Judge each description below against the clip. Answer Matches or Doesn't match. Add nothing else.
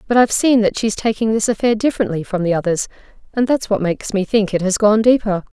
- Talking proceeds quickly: Matches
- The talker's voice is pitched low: Doesn't match